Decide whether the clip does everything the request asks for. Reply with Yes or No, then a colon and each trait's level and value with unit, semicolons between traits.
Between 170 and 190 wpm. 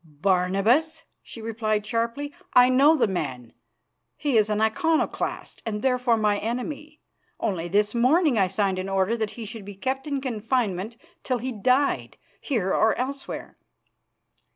No: average, 150 wpm